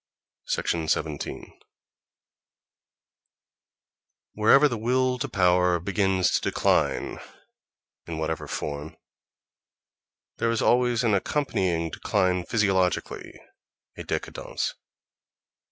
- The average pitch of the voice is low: Yes, very low, 95 Hz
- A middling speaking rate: No, slow, 80 wpm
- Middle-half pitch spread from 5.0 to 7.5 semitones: Yes, wide, 5.4 semitones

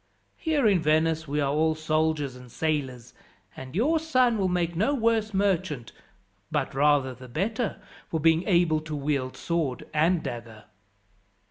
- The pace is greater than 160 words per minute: No, average, 150 wpm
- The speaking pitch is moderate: Yes, medium, 160 Hz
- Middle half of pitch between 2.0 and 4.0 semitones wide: No, wide, 5.4 semitones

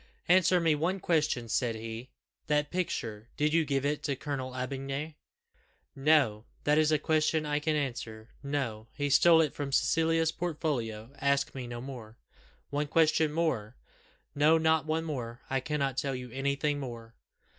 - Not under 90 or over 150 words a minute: No, average, 165 wpm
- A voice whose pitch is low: No, medium, 145 Hz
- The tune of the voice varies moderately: Yes, average, 3.6 semitones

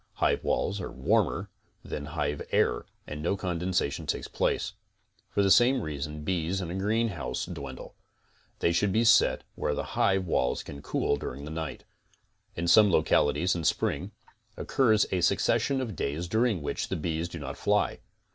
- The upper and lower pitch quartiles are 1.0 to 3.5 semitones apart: No, average, 4.8 semitones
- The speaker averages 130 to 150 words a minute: No, average, 170 wpm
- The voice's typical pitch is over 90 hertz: No, very low, 85 Hz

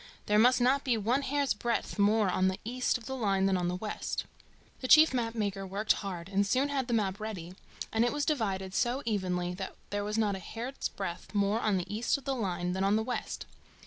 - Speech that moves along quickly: Yes, fast, 235 wpm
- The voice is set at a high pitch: Yes, high, 210 Hz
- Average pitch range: Yes, average, 4.1 semitones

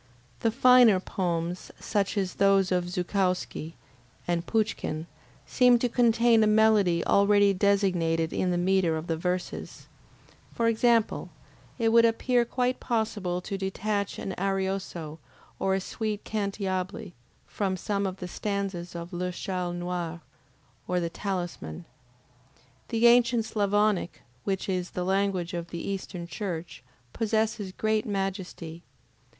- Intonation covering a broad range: No, average, 3.3 semitones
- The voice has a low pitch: No, high, 195 Hz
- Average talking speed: No, slow, 130 wpm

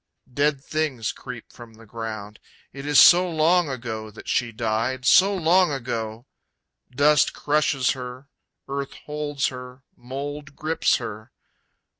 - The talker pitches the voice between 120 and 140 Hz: Yes, low, 135 Hz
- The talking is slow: Yes, slow, 130 wpm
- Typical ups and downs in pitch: Yes, average, 4.3 semitones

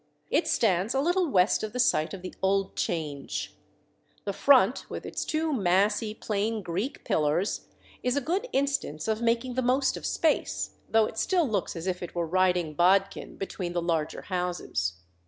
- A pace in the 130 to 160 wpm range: No, average, 175 wpm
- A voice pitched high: Yes, high, 200 Hz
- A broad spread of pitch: Yes, wide, 6.1 semitones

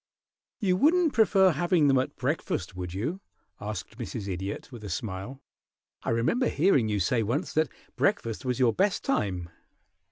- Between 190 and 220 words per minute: No, average, 160 wpm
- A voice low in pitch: Yes, low, 125 Hz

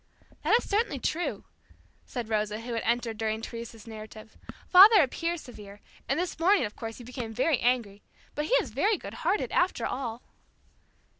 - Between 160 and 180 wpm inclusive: Yes, average, 170 wpm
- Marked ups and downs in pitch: Yes, wide, 7.0 semitones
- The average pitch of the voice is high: Yes, high, 240 Hz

